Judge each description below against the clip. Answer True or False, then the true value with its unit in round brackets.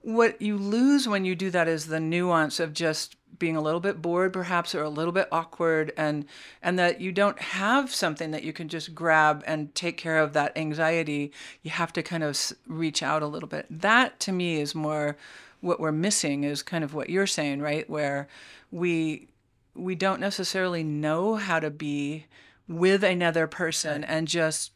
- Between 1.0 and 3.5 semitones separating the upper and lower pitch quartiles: True (2.9 semitones)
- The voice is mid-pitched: True (165 Hz)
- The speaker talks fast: False (195 wpm)